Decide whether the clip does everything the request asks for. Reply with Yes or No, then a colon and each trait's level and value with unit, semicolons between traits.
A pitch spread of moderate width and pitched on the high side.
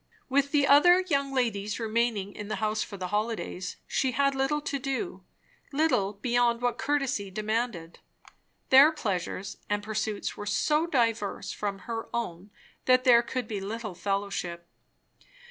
Yes: average, 4.8 semitones; high, 230 Hz